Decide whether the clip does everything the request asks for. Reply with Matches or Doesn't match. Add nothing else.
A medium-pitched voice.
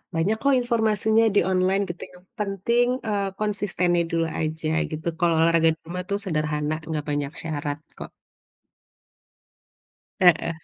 Matches